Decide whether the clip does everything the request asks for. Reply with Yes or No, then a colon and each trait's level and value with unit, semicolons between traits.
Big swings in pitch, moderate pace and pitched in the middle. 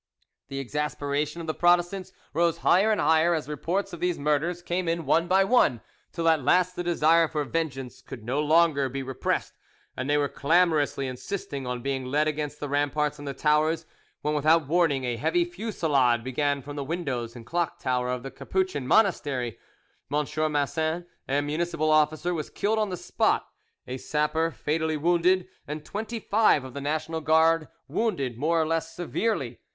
No: average, 3.4 semitones; average, 180 wpm; medium, 155 Hz